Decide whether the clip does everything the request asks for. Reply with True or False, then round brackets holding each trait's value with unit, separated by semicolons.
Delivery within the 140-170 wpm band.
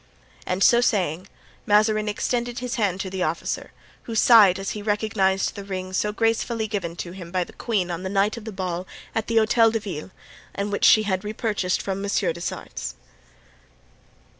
False (190 wpm)